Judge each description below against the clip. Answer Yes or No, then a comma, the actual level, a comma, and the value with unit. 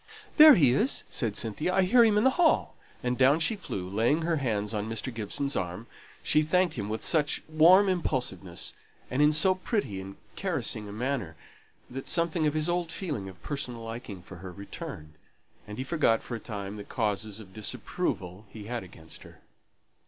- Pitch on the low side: Yes, low, 125 Hz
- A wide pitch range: Yes, wide, 7.8 semitones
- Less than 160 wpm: No, average, 190 wpm